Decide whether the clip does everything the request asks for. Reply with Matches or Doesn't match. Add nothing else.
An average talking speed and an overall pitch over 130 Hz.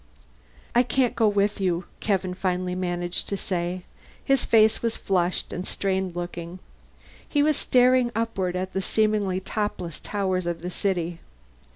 Matches